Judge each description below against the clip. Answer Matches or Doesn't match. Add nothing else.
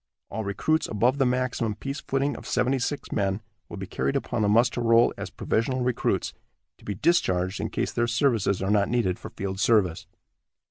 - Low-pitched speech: Matches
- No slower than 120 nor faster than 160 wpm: Doesn't match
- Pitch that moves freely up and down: Doesn't match